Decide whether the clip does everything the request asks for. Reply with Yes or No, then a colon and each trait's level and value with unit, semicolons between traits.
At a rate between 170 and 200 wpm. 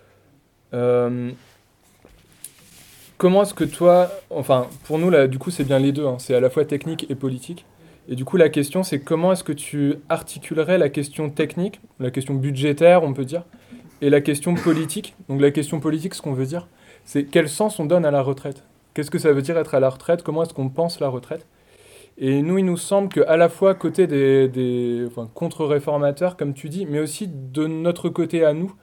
No: average, 210 wpm